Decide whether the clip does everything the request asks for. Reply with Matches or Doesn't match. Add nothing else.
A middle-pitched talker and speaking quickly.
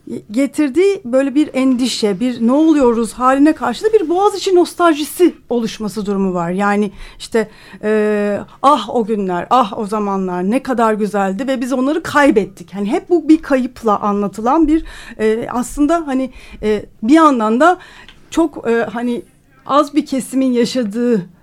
Doesn't match